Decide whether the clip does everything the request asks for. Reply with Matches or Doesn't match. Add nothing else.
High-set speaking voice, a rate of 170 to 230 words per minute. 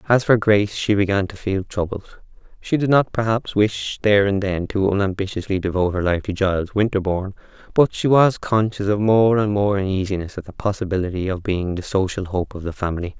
Doesn't match